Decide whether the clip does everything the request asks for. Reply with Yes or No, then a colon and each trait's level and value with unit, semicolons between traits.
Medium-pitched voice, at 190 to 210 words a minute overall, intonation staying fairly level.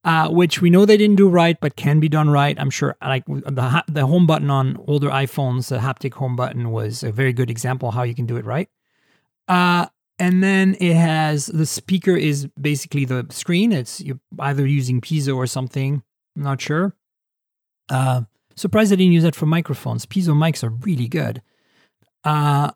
No: medium, 145 Hz; average, 200 wpm; average, 4.5 semitones